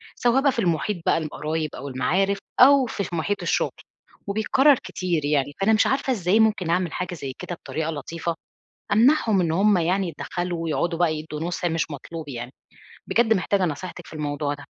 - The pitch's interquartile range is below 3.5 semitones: No, average, 4.7 semitones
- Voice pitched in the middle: Yes, medium, 175 Hz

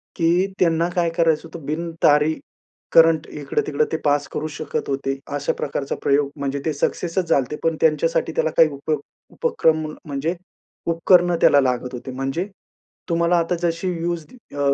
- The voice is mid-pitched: Yes, medium, 160 Hz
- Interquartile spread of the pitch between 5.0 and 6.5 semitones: No, average, 2.9 semitones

